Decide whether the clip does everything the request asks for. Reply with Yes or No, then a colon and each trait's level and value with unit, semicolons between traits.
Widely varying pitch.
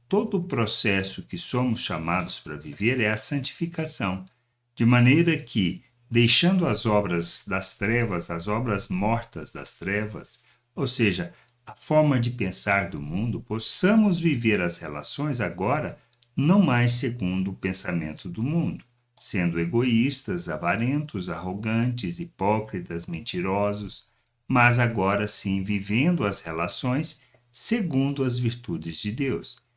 No: average, 4.9 semitones